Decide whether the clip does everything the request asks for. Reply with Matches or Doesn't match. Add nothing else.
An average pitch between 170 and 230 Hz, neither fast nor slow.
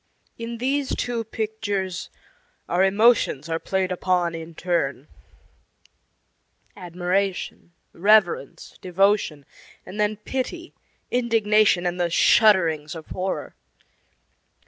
Doesn't match